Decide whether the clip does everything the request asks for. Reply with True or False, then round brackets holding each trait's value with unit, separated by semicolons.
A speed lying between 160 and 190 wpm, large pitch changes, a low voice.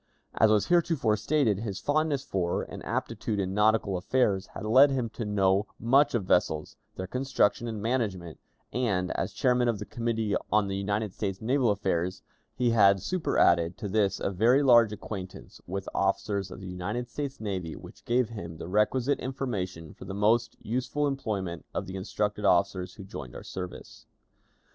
False (170 wpm; 4.2 semitones; 105 Hz)